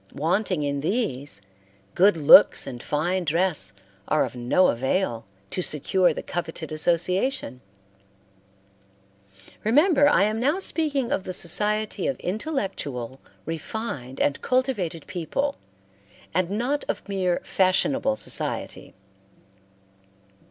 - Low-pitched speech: No, medium, 185 Hz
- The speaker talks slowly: Yes, slow, 110 wpm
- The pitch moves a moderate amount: No, wide, 7.0 semitones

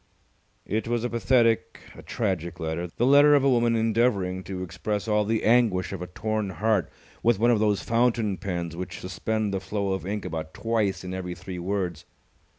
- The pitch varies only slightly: No, average, 3.8 semitones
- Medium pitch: No, low, 100 Hz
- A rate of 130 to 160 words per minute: No, average, 190 wpm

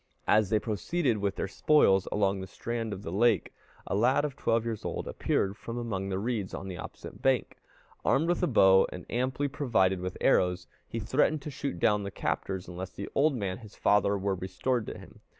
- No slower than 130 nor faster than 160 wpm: No, fast, 205 wpm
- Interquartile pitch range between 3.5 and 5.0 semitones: Yes, average, 4.6 semitones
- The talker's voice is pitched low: Yes, low, 105 Hz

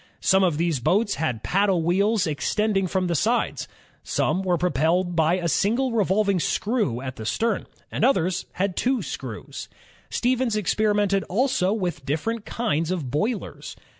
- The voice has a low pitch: No, high, 190 Hz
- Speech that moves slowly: No, average, 150 wpm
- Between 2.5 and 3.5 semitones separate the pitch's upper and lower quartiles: No, average, 4.3 semitones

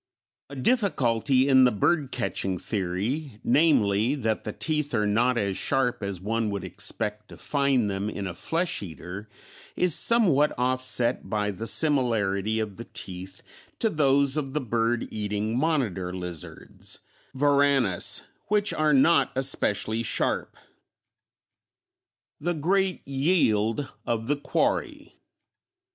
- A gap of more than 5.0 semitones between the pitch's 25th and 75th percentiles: Yes, wide, 5.6 semitones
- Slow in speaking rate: Yes, slow, 125 wpm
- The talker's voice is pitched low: Yes, low, 120 Hz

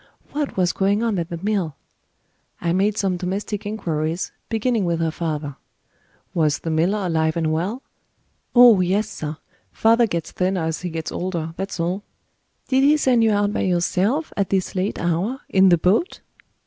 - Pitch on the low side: No, medium, 185 Hz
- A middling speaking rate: Yes, average, 175 wpm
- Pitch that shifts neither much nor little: Yes, average, 4.1 semitones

